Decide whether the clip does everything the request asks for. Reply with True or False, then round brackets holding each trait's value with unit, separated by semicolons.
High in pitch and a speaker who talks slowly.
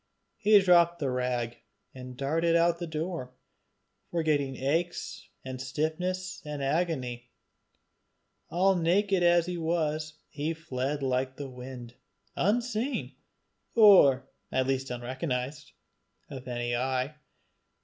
False (150 Hz; 115 wpm)